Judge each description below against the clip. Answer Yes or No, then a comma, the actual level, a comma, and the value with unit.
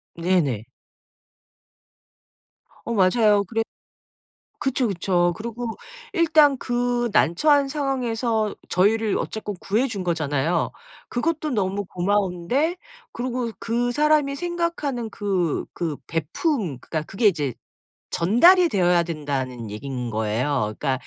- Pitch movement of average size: No, wide, 6.9 semitones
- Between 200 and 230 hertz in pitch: Yes, high, 210 Hz